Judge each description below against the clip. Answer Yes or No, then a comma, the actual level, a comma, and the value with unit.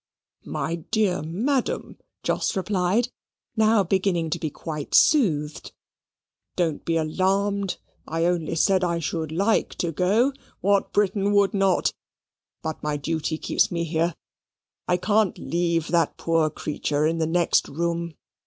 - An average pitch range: Yes, average, 3.4 semitones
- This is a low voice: No, medium, 170 Hz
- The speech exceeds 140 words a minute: No, slow, 135 wpm